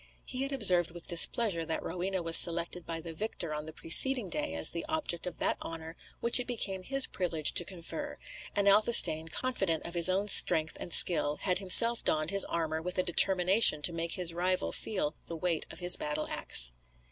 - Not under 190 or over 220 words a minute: Yes, average, 200 wpm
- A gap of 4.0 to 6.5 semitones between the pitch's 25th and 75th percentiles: No, average, 3.2 semitones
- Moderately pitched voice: Yes, medium, 175 Hz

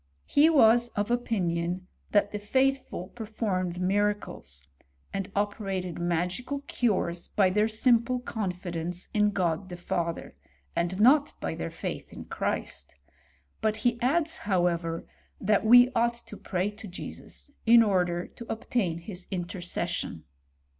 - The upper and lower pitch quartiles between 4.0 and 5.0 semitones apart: Yes, average, 4.7 semitones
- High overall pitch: Yes, high, 200 Hz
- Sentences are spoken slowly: Yes, slow, 130 wpm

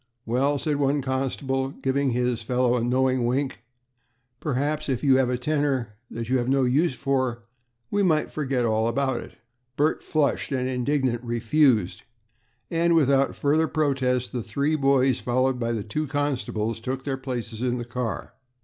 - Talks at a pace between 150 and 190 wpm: Yes, average, 165 wpm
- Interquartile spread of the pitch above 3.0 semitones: No, narrow, 2.4 semitones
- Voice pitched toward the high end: No, low, 130 Hz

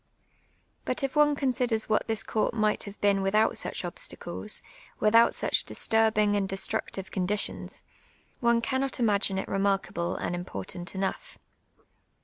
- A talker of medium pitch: No, high, 215 Hz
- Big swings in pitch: No, average, 3.2 semitones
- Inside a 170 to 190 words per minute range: No, slow, 135 wpm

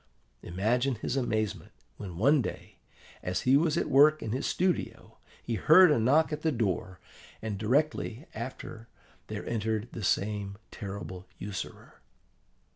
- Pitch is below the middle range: Yes, low, 115 Hz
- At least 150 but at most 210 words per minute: No, average, 140 wpm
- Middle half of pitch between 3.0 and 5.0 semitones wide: No, wide, 5.5 semitones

